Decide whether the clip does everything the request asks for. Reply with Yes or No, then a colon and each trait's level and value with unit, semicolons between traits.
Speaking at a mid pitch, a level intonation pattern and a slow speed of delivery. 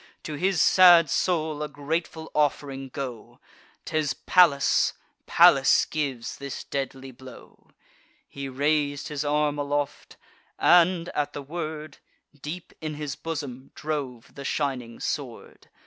Yes: medium, 145 Hz; narrow, 2.2 semitones; slow, 120 wpm